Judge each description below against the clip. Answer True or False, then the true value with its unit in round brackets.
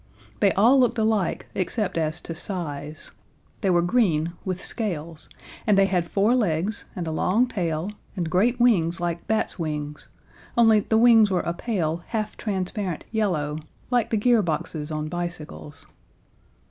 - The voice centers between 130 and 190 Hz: True (185 Hz)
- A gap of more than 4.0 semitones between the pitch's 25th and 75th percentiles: True (5.1 semitones)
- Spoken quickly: False (155 wpm)